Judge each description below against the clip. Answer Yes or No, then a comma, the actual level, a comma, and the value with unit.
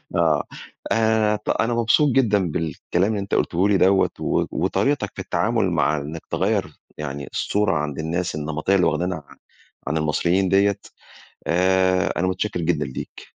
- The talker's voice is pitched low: Yes, very low, 95 Hz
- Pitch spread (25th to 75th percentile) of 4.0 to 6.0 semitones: Yes, average, 4.3 semitones